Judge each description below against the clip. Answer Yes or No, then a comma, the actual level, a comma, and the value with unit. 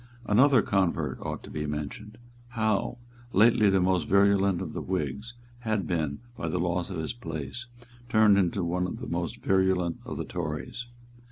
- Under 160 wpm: No, average, 170 wpm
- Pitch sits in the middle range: No, very low, 95 Hz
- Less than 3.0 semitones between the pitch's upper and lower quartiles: No, average, 3.9 semitones